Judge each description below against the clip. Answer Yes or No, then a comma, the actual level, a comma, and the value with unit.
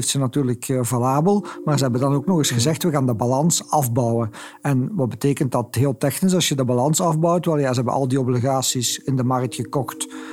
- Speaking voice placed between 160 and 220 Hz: No, low, 135 Hz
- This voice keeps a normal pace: No, fast, 220 wpm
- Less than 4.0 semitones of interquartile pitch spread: Yes, average, 3.2 semitones